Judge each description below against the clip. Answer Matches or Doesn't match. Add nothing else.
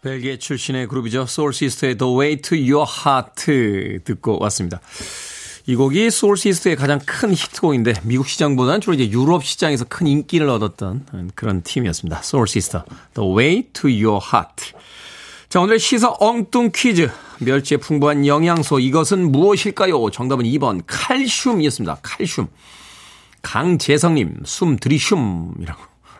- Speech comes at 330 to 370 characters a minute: Matches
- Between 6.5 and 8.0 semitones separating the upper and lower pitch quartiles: Doesn't match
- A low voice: Doesn't match